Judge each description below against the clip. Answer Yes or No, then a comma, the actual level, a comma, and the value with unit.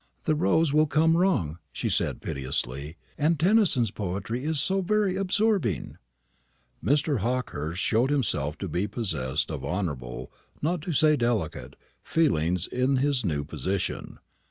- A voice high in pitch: No, low, 125 Hz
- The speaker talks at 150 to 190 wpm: No, slow, 135 wpm